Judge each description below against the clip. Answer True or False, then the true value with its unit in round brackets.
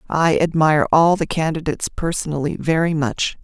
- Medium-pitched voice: True (155 Hz)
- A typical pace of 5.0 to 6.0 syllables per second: True (5.3 syllables/s)